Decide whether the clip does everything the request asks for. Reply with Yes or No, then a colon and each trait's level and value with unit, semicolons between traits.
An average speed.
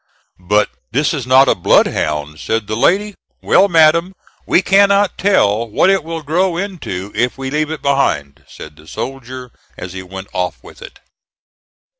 Yes: average, 165 wpm